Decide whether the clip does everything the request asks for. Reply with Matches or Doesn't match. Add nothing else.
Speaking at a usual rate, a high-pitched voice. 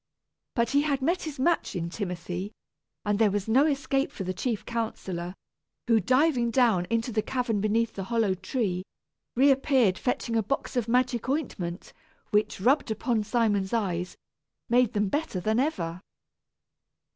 Matches